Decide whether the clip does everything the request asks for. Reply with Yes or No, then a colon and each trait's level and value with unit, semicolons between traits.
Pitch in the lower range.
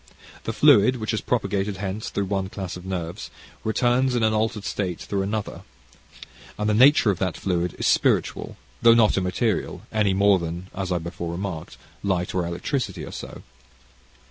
Yes: low, 100 Hz